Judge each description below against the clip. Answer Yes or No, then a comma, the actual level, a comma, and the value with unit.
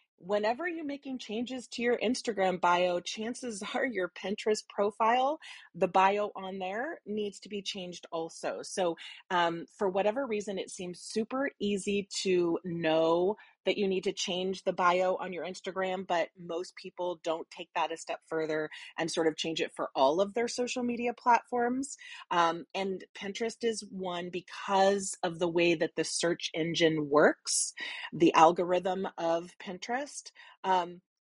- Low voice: No, high, 190 Hz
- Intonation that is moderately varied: Yes, average, 4.6 semitones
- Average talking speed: Yes, average, 160 wpm